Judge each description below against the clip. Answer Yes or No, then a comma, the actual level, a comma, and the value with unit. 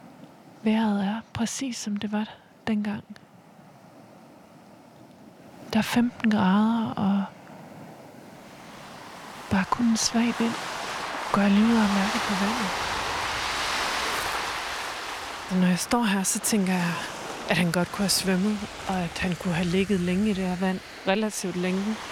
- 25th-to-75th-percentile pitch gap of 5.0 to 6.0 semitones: No, average, 2.9 semitones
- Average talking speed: No, slow, 135 wpm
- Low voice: No, high, 205 Hz